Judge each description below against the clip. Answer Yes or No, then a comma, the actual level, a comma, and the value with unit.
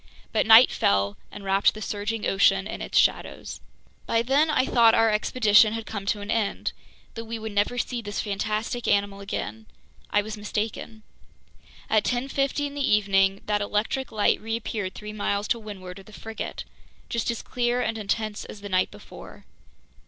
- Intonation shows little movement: Yes, narrow, 2.0 semitones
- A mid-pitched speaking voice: No, high, 215 Hz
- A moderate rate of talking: Yes, average, 175 wpm